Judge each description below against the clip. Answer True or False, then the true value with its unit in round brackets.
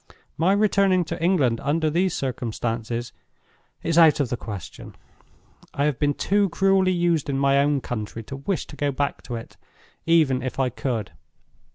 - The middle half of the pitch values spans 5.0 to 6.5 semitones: True (5.5 semitones)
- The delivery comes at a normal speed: True (170 wpm)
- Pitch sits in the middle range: True (145 Hz)